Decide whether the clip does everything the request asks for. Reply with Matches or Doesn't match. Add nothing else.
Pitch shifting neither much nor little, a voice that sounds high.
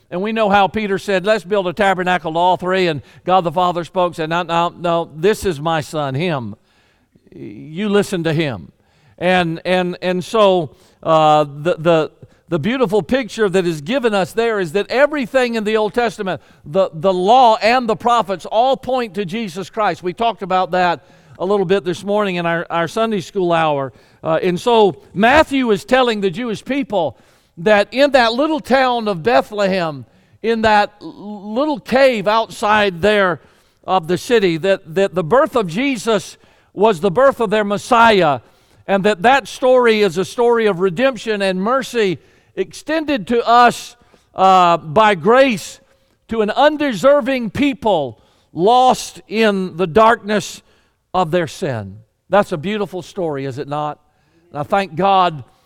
Matches